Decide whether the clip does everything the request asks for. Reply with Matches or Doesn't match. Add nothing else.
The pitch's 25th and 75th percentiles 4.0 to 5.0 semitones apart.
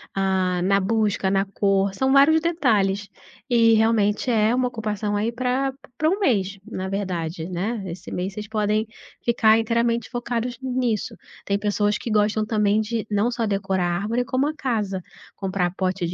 Doesn't match